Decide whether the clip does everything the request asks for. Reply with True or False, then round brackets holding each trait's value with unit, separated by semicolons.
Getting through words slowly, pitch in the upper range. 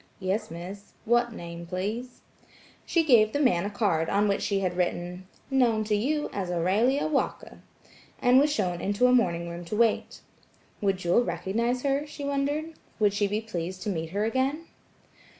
False (175 wpm; 210 Hz)